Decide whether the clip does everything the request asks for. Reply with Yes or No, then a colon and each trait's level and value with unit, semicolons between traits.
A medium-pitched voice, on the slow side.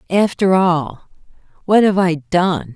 Yes: medium, 180 Hz; slow, 130 wpm